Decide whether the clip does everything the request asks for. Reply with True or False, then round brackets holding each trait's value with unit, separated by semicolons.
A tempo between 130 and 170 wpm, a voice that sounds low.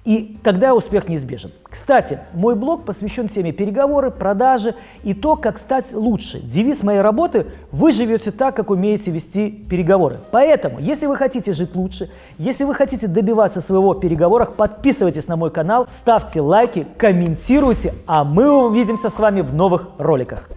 False (160 wpm; 210 Hz)